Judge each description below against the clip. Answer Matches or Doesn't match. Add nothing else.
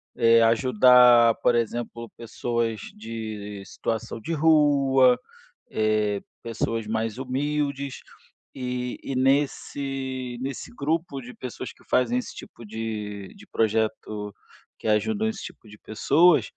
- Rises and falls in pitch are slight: Doesn't match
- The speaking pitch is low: Matches